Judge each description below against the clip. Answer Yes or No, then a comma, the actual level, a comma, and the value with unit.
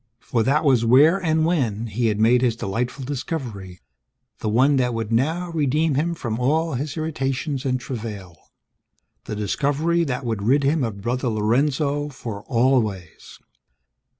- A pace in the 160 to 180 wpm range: No, average, 150 wpm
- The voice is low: Yes, low, 130 Hz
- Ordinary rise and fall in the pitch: Yes, average, 4.5 semitones